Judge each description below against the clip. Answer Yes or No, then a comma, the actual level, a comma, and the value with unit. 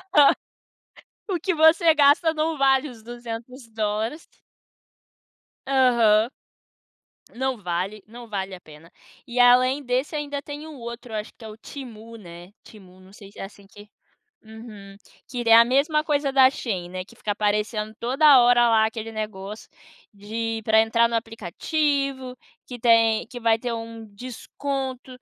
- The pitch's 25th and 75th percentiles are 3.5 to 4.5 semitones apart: Yes, average, 3.8 semitones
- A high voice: Yes, high, 230 Hz